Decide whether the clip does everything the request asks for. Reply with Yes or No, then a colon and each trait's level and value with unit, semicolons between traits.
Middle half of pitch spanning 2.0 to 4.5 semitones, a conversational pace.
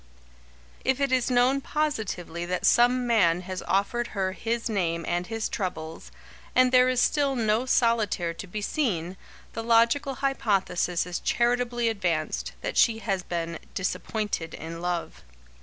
No: wide, 5.5 semitones; average, 145 wpm